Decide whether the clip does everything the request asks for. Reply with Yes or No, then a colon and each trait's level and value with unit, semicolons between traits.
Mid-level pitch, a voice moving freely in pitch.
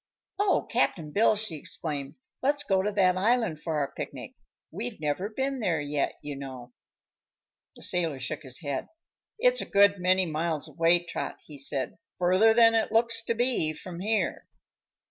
Yes: medium, 180 Hz; wide, 6.7 semitones